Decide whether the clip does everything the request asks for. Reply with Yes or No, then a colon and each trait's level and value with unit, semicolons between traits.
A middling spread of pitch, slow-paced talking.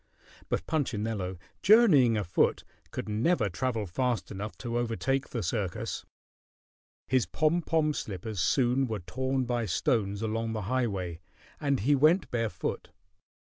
Yes: average, 4.4 semitones; slow, 130 wpm